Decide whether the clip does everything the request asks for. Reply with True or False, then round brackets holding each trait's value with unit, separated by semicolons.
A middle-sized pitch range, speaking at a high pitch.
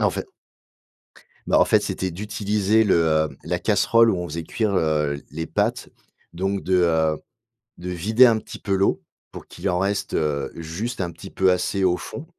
False (4.0 semitones; 90 Hz)